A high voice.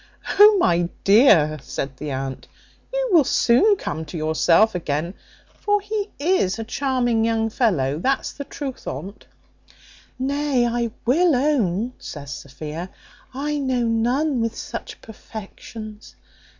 Yes: high, 230 Hz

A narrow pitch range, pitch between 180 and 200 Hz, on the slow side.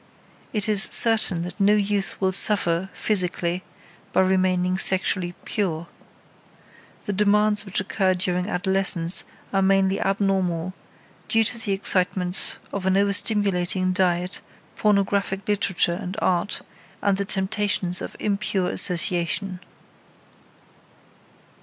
Yes: narrow, 1.9 semitones; high, 190 Hz; slow, 110 wpm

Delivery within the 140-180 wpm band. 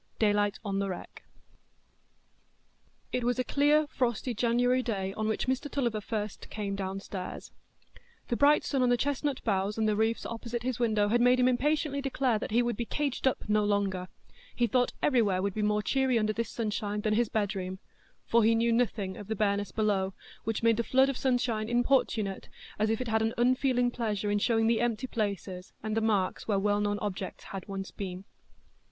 No: average, 195 wpm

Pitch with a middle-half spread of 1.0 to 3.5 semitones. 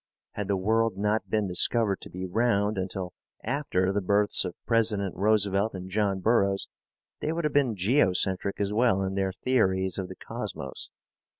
Yes: average, 2.8 semitones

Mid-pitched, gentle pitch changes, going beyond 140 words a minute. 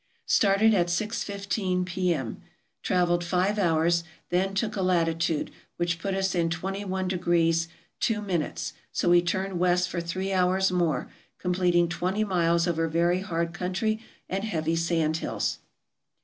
No: medium, 180 Hz; narrow, 2.2 semitones; slow, 135 wpm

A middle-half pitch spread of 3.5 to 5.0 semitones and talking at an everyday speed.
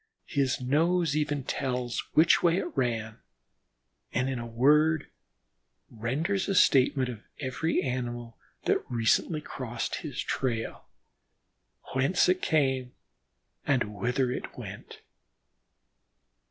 No: average, 4.0 semitones; slow, 110 wpm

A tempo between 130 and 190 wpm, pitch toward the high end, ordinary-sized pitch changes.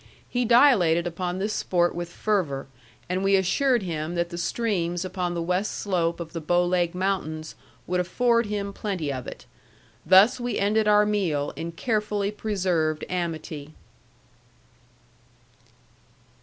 No: average, 140 wpm; medium, 180 Hz; average, 3.6 semitones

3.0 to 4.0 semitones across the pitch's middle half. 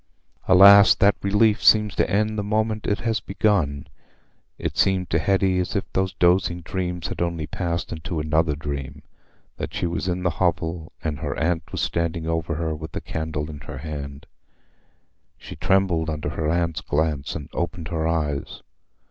Yes: average, 3.3 semitones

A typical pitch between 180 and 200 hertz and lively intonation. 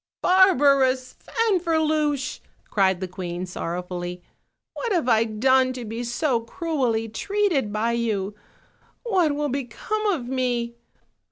No: very high, 255 Hz; wide, 6.1 semitones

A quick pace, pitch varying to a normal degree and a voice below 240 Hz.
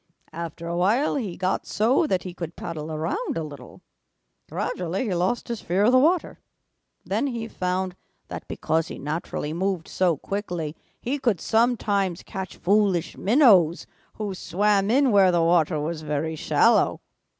No: average, 160 wpm; average, 4.5 semitones; medium, 185 Hz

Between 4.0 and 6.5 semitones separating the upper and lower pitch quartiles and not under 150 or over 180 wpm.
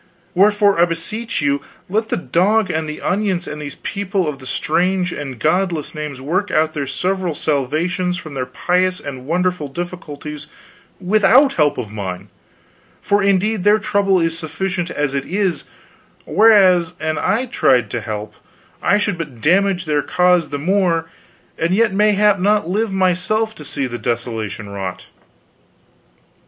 Yes: average, 5.1 semitones; average, 155 wpm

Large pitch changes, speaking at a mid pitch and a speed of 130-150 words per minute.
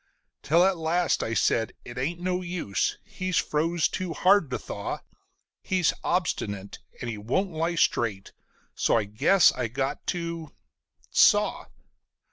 Yes: wide, 7.1 semitones; medium, 160 Hz; average, 140 wpm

